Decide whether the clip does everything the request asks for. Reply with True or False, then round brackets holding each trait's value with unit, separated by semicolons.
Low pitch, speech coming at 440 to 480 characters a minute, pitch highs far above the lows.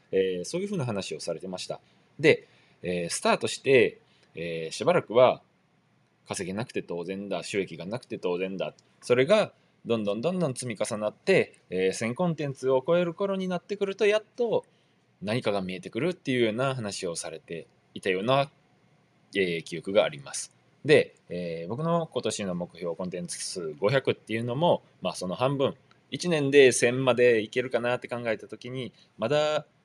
False (125 Hz; 340 characters per minute; 8.8 semitones)